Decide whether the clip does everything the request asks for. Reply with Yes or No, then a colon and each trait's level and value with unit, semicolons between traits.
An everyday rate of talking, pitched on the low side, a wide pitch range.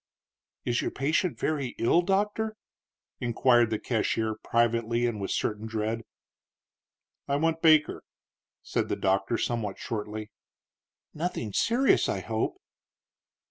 No: slow, 120 wpm; low, 120 Hz; wide, 6.4 semitones